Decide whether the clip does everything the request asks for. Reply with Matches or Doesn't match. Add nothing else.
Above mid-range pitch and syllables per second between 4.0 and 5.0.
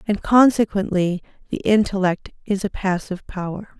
Matches